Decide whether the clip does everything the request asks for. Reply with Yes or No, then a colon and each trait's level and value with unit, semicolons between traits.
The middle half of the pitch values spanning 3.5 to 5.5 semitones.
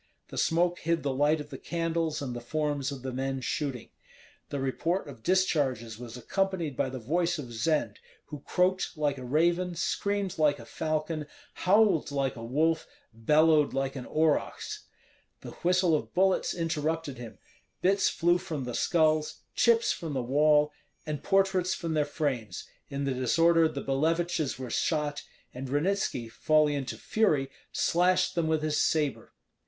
Yes: average, 3.8 semitones